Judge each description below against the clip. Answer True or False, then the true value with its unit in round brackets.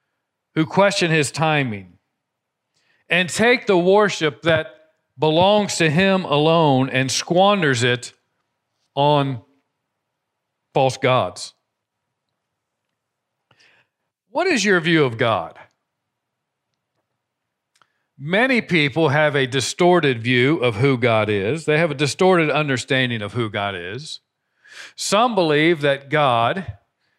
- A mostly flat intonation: False (4.9 semitones)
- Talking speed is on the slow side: True (105 wpm)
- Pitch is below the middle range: False (150 Hz)